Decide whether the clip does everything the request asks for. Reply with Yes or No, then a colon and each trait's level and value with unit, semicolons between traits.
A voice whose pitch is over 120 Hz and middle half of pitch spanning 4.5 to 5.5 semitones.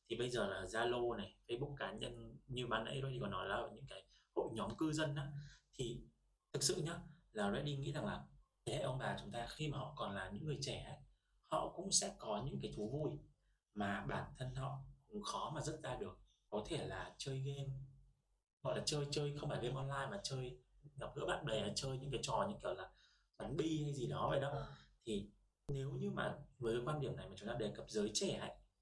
Yes: low, 135 Hz; average, 4.9 semitones